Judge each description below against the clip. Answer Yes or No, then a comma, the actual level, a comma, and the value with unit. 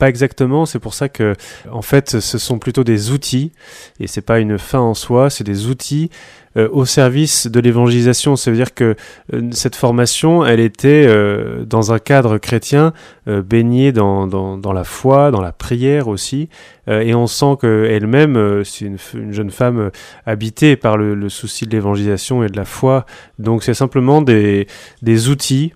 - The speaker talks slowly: No, average, 190 wpm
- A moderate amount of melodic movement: Yes, average, 4.1 semitones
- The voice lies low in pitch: Yes, low, 120 Hz